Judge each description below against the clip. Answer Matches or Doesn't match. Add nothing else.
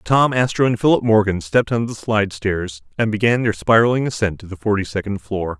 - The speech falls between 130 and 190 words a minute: Doesn't match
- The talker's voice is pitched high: Doesn't match